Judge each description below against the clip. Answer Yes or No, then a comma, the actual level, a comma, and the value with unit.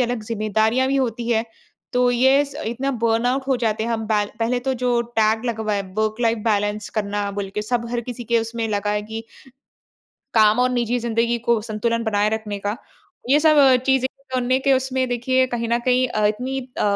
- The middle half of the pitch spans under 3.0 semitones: Yes, narrow, 2.5 semitones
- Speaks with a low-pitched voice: No, high, 230 Hz